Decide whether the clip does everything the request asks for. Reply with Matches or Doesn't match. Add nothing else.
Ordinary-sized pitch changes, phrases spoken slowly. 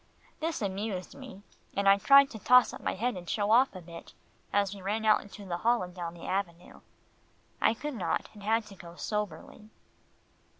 Doesn't match